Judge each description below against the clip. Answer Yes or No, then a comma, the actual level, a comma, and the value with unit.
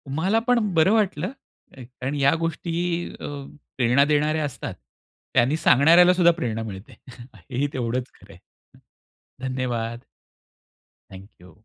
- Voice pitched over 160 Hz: No, medium, 140 Hz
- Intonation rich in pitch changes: Yes, wide, 5.8 semitones